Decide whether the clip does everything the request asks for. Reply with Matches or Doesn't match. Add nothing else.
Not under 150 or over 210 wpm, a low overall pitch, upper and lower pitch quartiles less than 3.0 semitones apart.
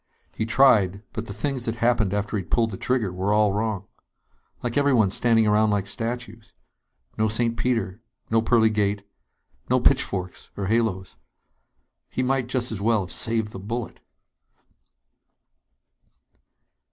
Doesn't match